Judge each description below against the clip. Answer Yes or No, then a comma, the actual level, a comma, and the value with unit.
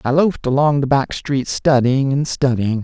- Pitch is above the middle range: No, low, 135 Hz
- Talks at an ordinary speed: Yes, average, 190 wpm